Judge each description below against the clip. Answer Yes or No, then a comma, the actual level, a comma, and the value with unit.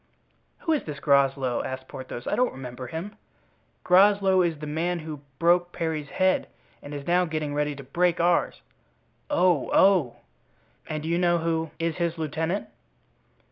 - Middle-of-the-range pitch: Yes, medium, 160 Hz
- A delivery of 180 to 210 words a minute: No, average, 160 wpm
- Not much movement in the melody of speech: No, average, 3.5 semitones